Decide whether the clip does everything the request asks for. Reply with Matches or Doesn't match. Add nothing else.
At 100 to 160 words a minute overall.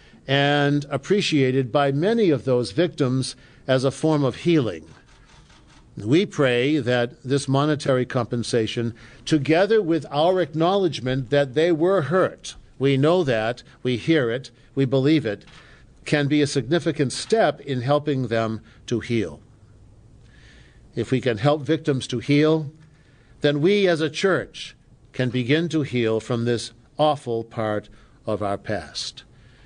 Matches